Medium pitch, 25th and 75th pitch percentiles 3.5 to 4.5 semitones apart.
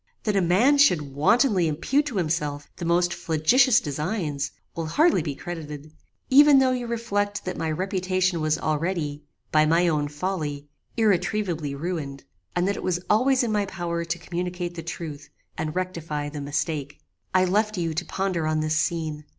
Yes: medium, 170 Hz; average, 4.2 semitones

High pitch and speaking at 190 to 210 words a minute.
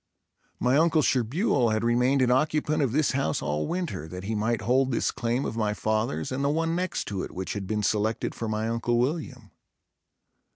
No: low, 120 Hz; average, 200 wpm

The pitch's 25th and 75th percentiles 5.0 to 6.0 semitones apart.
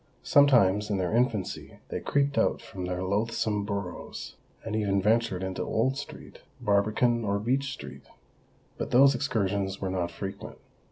No: average, 3.8 semitones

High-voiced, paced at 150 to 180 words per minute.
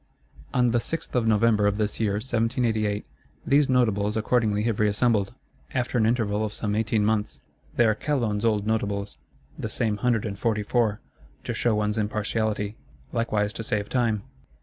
No: low, 110 Hz; average, 160 wpm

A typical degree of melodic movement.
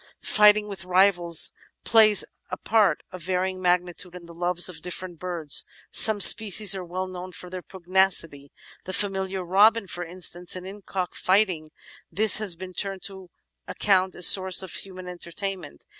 No: narrow, 1.7 semitones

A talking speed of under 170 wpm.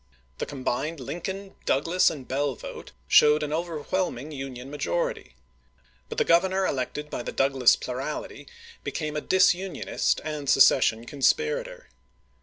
Yes: average, 140 wpm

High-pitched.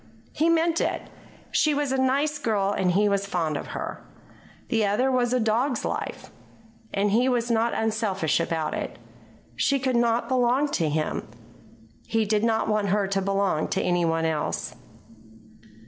Yes: high, 220 Hz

